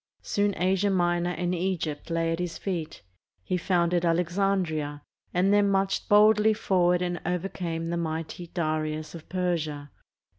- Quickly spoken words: No, average, 140 wpm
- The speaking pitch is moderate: Yes, medium, 175 Hz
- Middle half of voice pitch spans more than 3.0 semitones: No, narrow, 2.4 semitones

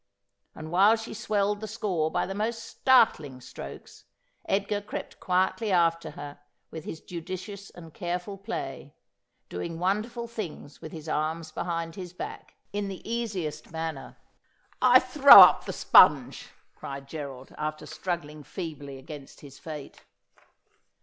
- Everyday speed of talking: Yes, average, 145 wpm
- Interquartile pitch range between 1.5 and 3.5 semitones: No, average, 4.9 semitones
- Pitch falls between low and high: Yes, medium, 170 Hz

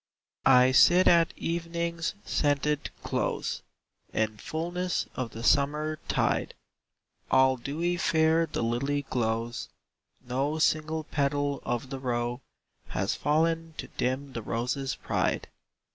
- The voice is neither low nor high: Yes, medium, 145 Hz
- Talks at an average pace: No, slow, 120 wpm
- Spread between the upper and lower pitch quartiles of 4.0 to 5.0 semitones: Yes, average, 4.3 semitones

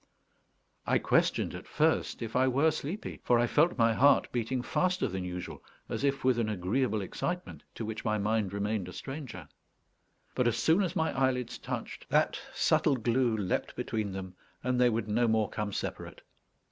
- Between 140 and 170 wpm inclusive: No, average, 180 wpm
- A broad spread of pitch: No, average, 3.8 semitones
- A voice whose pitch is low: Yes, low, 120 Hz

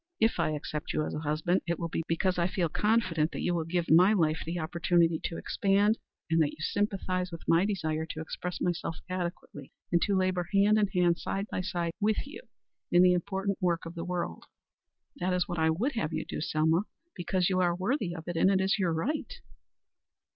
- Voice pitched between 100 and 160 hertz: No, medium, 175 Hz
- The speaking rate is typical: No, fast, 220 wpm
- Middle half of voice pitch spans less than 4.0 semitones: Yes, narrow, 2.6 semitones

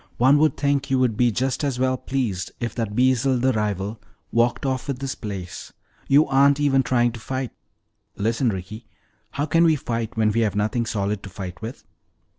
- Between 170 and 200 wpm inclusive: Yes, average, 195 wpm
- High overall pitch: No, low, 120 Hz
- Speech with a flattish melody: No, average, 3.8 semitones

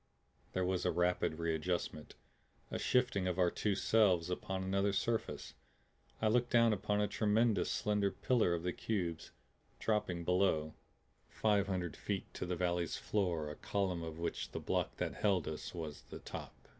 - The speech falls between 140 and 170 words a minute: Yes, average, 165 wpm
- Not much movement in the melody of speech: No, average, 3.3 semitones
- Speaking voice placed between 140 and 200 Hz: No, very low, 95 Hz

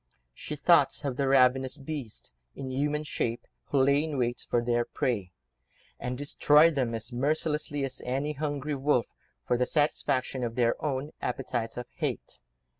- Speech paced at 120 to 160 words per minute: Yes, average, 150 wpm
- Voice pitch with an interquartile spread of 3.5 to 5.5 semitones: No, average, 3.0 semitones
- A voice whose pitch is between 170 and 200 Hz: No, low, 135 Hz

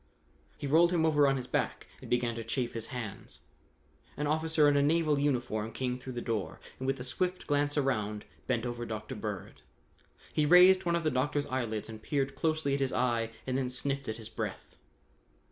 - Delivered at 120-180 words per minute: No, average, 200 wpm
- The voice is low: Yes, low, 130 Hz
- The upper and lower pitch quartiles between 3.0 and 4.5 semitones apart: Yes, average, 3.7 semitones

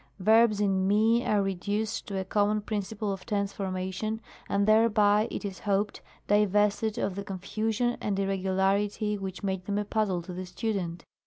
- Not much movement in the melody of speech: Yes, narrow, 1.9 semitones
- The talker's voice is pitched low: No, high, 205 Hz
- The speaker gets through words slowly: No, average, 165 wpm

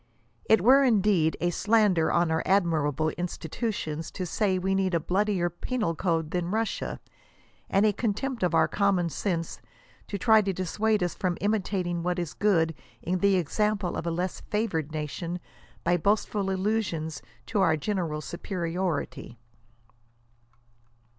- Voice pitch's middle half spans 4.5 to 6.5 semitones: No, average, 3.7 semitones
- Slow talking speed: No, average, 145 wpm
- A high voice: No, medium, 180 Hz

